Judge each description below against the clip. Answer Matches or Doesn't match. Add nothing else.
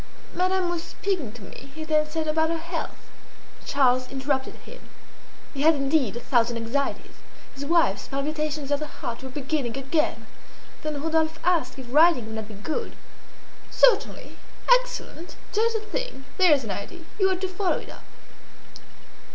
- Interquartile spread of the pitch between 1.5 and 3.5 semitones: Doesn't match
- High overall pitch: Matches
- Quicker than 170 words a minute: Doesn't match